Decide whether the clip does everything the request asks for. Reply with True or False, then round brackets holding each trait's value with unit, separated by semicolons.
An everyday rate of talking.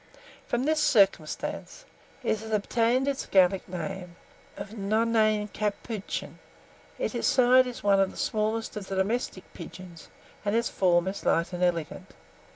True (150 wpm)